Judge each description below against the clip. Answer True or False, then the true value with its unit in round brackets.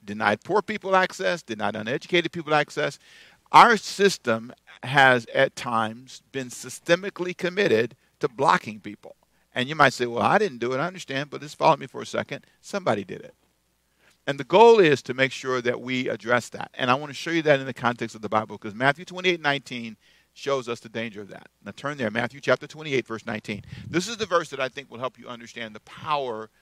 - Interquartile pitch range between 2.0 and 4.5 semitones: False (5.1 semitones)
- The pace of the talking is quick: True (215 wpm)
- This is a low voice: True (130 Hz)